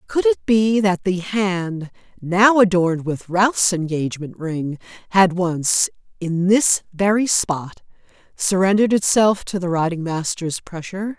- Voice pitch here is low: No, medium, 185 Hz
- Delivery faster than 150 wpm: No, slow, 135 wpm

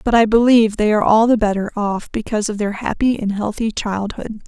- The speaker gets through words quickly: Yes, fast, 215 wpm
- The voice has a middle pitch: No, high, 215 Hz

